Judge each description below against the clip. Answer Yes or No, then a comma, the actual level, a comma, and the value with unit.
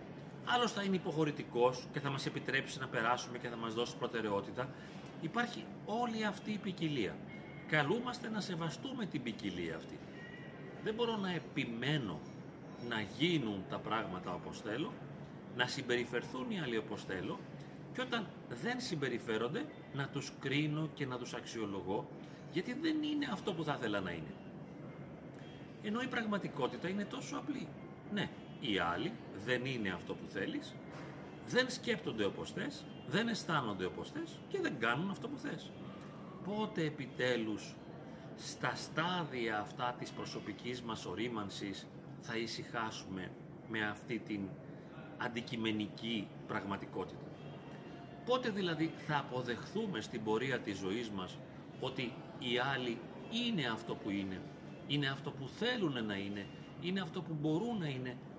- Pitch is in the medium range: Yes, medium, 145 Hz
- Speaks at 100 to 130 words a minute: No, average, 140 wpm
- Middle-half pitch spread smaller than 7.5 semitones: No, wide, 7.8 semitones